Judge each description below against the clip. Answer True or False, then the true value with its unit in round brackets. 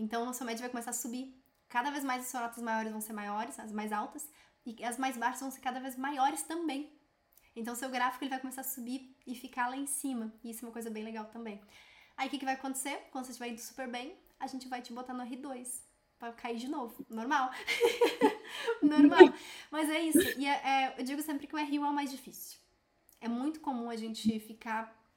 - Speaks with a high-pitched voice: True (255 Hz)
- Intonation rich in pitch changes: False (3.3 semitones)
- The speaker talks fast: True (235 wpm)